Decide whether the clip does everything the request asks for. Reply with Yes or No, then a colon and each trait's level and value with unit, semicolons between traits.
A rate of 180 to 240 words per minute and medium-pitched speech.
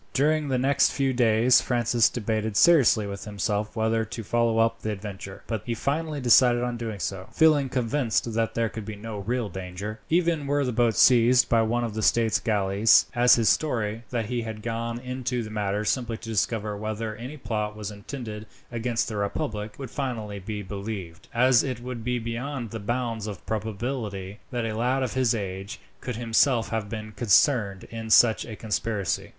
No: average, 190 wpm; low, 115 Hz